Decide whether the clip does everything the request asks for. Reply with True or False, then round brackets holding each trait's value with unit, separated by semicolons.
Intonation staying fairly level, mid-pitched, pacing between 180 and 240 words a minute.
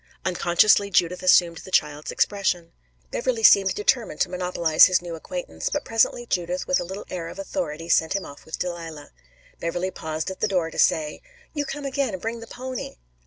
False (3.4 semitones; 180 Hz; 190 wpm)